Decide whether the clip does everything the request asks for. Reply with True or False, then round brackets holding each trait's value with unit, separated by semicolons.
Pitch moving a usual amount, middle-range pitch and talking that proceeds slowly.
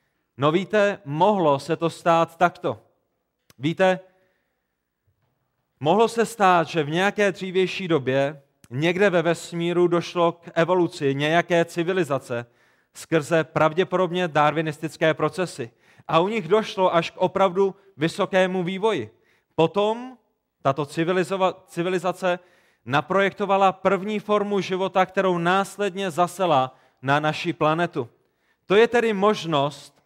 True (3.5 semitones; 175 Hz; 110 wpm)